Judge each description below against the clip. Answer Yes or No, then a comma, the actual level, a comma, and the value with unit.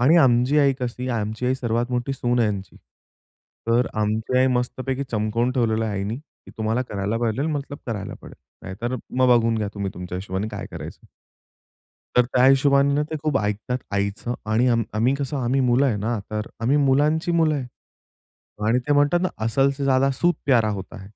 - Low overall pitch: Yes, low, 125 Hz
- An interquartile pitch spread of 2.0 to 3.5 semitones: No, average, 4.0 semitones